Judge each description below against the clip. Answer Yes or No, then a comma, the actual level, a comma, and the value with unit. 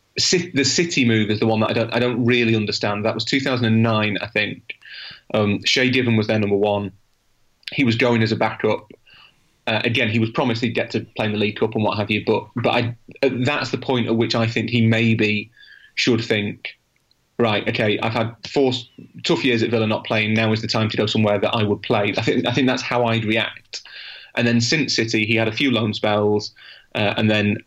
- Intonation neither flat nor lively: No, narrow, 2.1 semitones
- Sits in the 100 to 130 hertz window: Yes, low, 115 Hz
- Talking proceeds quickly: Yes, fast, 230 wpm